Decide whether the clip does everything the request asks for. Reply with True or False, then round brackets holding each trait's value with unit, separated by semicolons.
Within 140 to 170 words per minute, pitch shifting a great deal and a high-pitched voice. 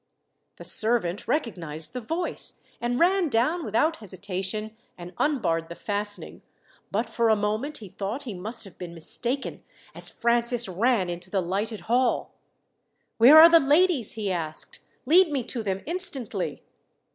True (150 wpm; 5.8 semitones; 225 Hz)